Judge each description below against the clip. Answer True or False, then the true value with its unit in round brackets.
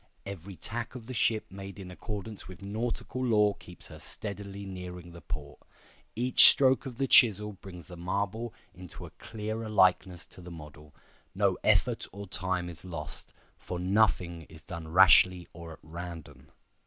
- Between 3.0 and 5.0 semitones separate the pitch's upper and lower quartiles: True (3.6 semitones)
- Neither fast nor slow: True (165 wpm)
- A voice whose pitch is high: False (95 Hz)